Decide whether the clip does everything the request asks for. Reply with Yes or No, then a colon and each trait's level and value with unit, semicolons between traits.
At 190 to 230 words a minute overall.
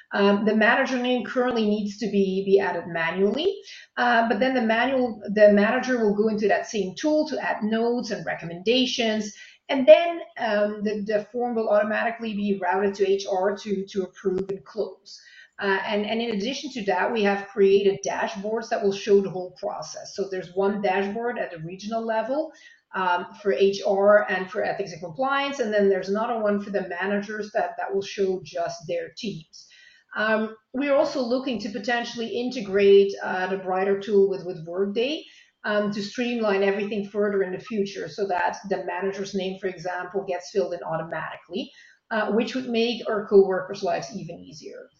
No: average, 180 wpm